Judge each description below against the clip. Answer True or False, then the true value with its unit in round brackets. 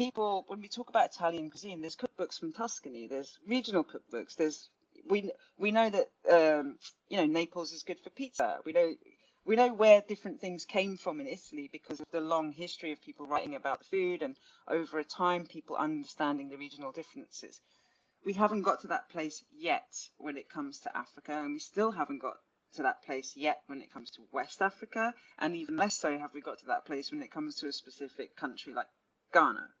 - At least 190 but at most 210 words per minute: True (205 wpm)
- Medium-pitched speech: True (175 Hz)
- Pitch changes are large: True (7.3 semitones)